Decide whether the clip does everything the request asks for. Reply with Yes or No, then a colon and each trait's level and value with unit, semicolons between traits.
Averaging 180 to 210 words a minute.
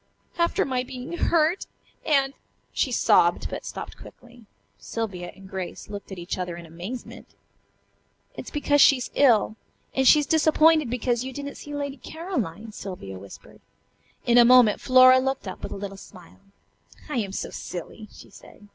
No: average, 165 wpm